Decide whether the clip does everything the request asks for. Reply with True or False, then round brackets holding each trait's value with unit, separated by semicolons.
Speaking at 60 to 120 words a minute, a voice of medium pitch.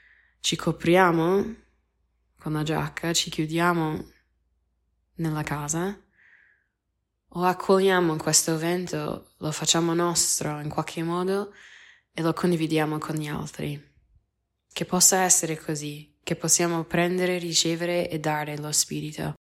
True (115 wpm; 165 Hz)